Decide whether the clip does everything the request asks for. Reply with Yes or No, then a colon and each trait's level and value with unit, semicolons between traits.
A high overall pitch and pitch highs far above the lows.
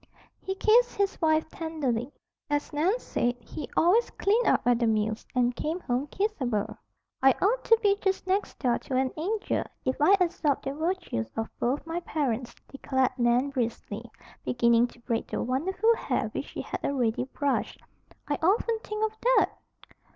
Yes: very high, 290 Hz; wide, 7.9 semitones